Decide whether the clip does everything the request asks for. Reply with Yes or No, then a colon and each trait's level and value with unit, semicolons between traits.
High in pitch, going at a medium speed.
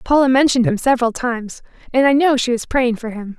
No: high, 245 Hz; fast, 230 wpm